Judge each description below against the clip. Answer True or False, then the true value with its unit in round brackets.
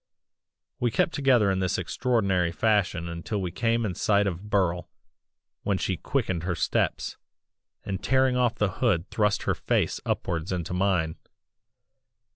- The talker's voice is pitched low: True (100 Hz)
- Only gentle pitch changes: False (4.3 semitones)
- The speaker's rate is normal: True (145 wpm)